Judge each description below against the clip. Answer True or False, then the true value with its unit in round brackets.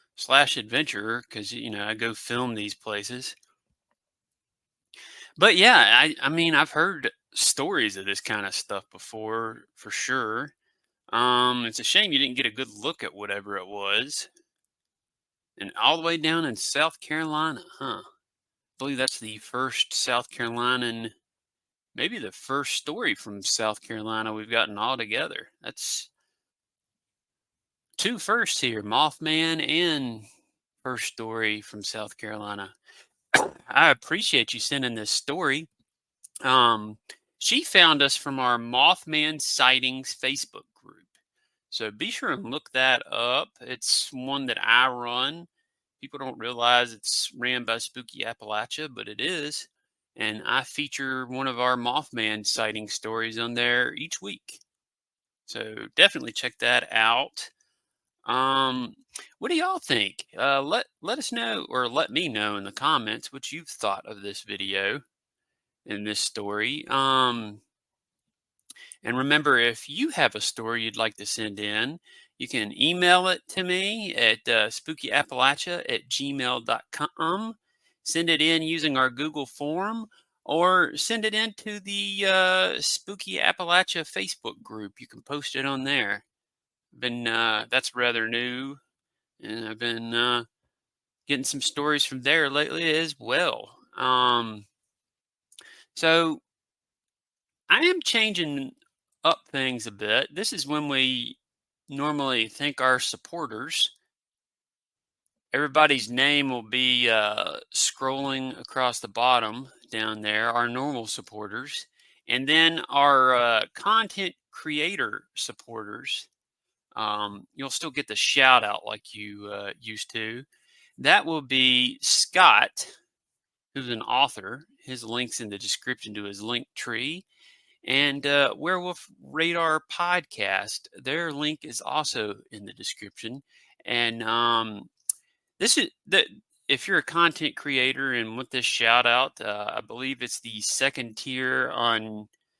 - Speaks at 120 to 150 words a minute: True (135 wpm)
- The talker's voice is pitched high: False (130 Hz)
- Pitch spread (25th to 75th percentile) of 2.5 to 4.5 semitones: False (5.2 semitones)